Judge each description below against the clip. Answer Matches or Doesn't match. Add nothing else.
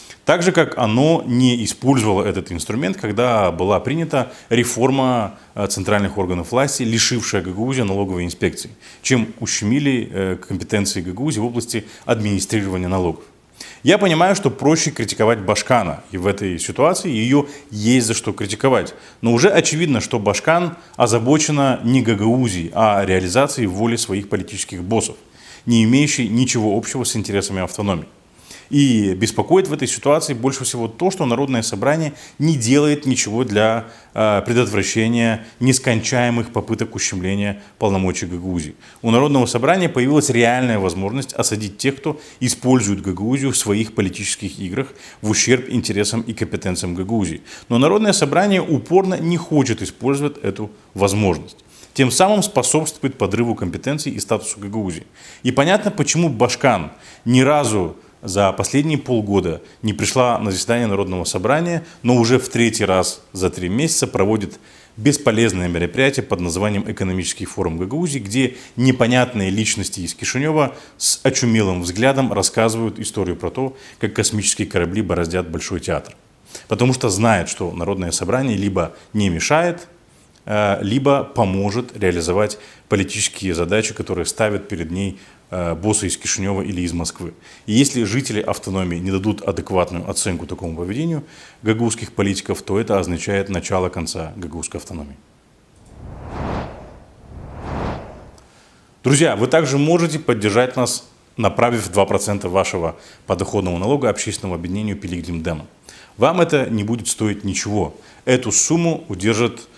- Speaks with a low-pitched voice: Matches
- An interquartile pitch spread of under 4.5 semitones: Doesn't match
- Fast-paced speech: Doesn't match